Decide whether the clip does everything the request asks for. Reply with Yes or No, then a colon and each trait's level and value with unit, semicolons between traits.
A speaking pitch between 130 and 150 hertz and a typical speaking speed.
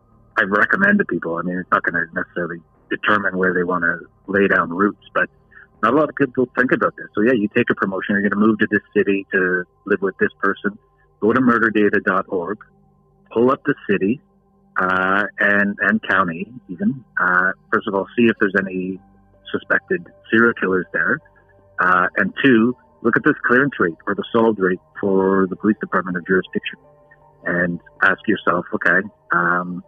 No: low, 100 Hz; average, 185 wpm